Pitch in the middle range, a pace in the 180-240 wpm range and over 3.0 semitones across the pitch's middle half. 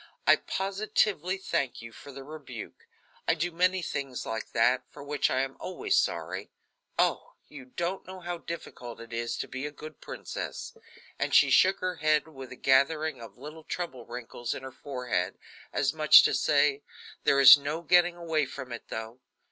Yes: medium, 145 Hz; average, 185 wpm; average, 4.7 semitones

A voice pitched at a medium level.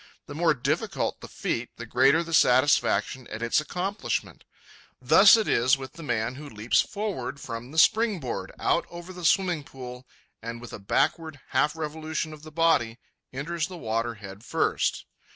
Yes: medium, 145 Hz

